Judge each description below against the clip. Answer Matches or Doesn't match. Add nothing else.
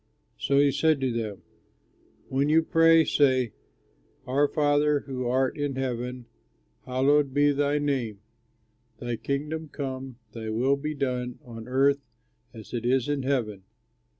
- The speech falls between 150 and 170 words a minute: Doesn't match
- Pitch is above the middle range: Doesn't match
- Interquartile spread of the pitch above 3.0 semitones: Doesn't match